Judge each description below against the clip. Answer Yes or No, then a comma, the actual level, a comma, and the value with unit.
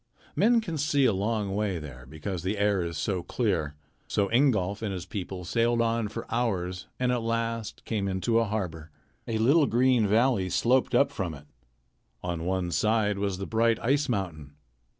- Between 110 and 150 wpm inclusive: No, average, 180 wpm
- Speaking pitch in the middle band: No, low, 105 Hz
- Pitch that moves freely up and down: No, average, 4.2 semitones